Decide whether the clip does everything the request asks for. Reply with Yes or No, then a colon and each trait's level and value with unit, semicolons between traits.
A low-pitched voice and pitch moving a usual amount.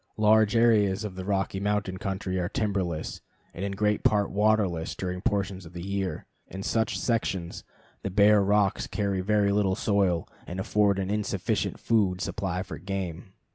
No: low, 100 Hz; narrow, 1.9 semitones